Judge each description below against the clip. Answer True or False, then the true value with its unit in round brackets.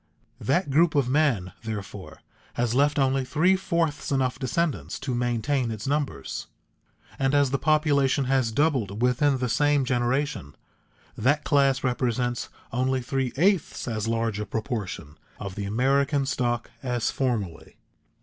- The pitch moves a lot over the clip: False (3.8 semitones)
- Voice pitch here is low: True (130 Hz)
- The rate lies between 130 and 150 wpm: True (140 wpm)